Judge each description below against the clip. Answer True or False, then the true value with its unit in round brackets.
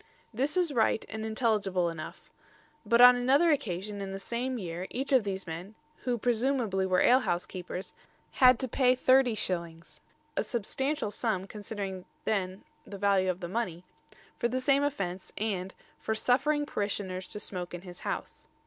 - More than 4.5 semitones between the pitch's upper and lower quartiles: True (5.1 semitones)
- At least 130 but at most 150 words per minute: False (160 wpm)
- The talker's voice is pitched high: True (210 Hz)